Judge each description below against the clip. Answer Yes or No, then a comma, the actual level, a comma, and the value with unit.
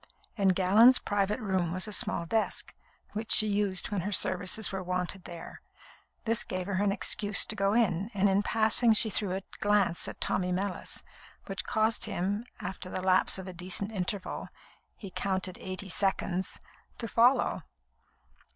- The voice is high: Yes, high, 195 Hz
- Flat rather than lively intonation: Yes, narrow, 2.2 semitones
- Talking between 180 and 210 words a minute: No, average, 165 wpm